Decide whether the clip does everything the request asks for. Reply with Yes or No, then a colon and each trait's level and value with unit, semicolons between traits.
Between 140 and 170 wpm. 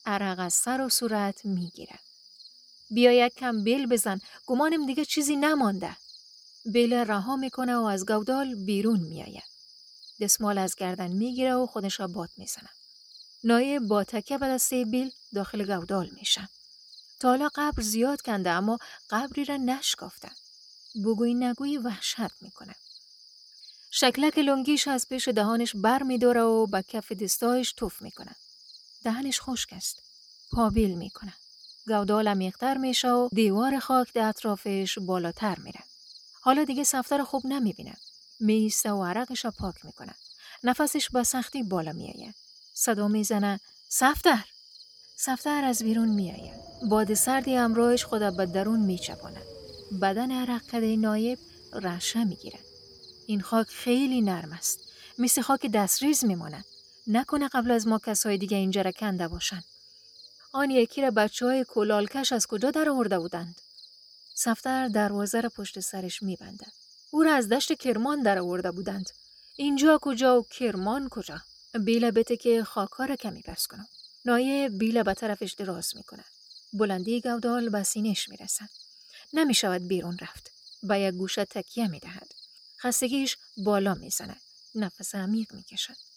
Yes: average, 150 wpm